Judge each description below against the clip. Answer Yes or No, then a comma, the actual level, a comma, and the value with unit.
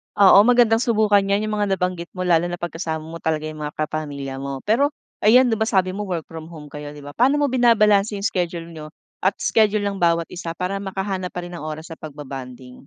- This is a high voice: No, medium, 180 Hz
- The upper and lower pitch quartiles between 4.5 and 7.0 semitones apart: Yes, average, 5.0 semitones